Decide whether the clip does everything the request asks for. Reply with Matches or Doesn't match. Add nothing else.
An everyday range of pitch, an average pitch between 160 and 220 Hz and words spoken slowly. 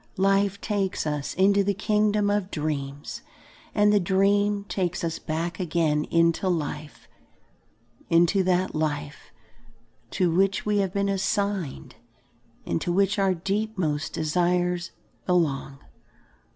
Matches